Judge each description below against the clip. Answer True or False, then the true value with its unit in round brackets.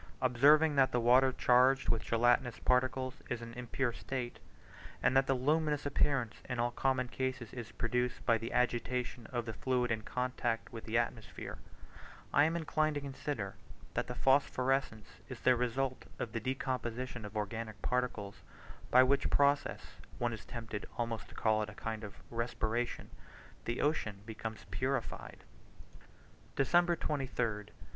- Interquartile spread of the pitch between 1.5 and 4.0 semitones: True (2.5 semitones)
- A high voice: False (125 Hz)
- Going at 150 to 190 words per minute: True (155 wpm)